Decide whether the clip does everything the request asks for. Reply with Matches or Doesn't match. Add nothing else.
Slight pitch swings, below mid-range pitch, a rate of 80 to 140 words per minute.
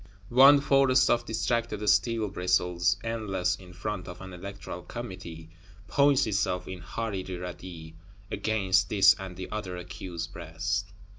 Doesn't match